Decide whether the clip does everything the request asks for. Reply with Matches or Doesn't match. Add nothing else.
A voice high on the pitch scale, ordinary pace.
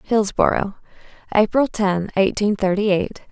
Doesn't match